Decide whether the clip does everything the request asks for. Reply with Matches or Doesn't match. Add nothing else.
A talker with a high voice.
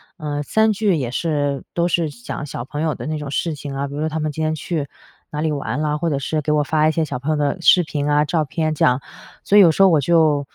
Doesn't match